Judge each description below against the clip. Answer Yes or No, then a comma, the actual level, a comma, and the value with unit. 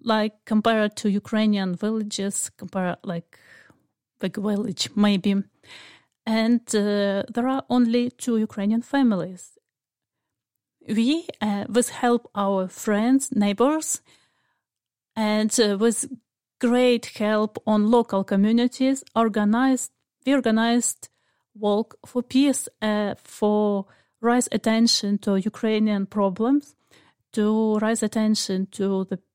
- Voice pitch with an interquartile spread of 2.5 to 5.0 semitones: Yes, average, 2.8 semitones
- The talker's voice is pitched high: Yes, high, 215 Hz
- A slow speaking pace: Yes, slow, 105 wpm